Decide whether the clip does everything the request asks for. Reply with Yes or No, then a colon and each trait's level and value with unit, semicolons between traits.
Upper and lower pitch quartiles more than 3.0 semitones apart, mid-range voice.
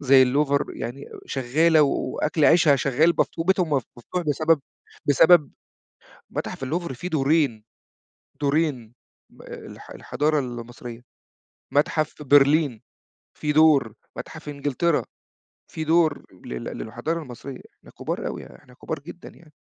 Yes: average, 3.6 semitones; medium, 145 Hz